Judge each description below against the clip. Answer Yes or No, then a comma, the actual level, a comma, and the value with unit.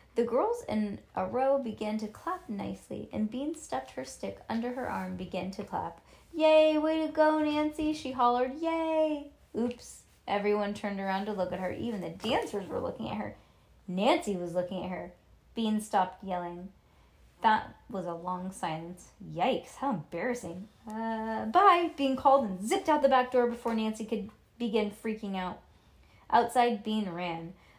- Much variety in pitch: Yes, wide, 6.5 semitones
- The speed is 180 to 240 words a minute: No, average, 170 wpm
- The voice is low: No, high, 220 Hz